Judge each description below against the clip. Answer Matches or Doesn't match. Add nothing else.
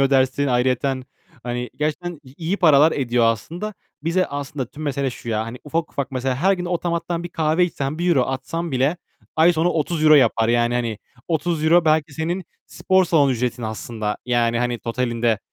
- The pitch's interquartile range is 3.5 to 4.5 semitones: Doesn't match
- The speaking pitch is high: Doesn't match